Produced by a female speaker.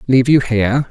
No: male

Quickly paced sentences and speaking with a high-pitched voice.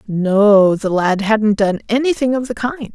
No: average, 185 wpm; high, 220 Hz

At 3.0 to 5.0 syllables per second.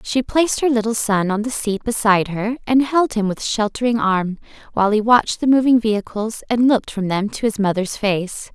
No: 5.5 syllables/s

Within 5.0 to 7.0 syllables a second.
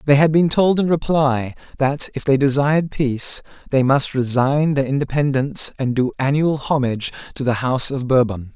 Yes: 5.2 syllables/s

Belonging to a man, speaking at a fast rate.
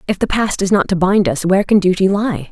No: female; fast, 285 wpm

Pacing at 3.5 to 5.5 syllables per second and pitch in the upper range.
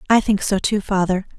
Yes: 5.4 syllables/s; high, 200 Hz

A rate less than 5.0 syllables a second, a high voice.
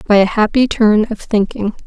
No: 5.1 syllables/s; high, 215 Hz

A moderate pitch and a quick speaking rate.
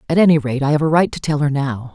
Yes: medium, 145 Hz; fast, 340 wpm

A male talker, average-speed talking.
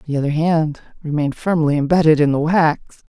No: female; average, 175 wpm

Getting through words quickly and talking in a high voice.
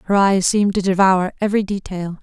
No: average, 190 wpm; high, 195 Hz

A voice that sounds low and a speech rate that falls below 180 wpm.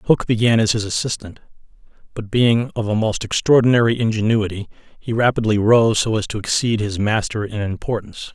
Yes: low, 110 Hz; average, 165 wpm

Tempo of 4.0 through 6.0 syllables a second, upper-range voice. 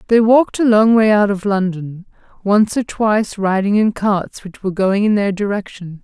Yes: 5.0 syllables/s; high, 205 Hz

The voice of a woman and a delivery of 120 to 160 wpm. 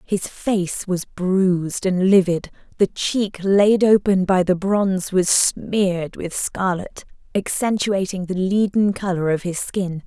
Yes: female; average, 145 wpm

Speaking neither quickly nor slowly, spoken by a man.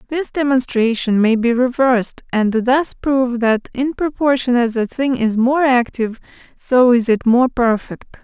No: average, 160 wpm; female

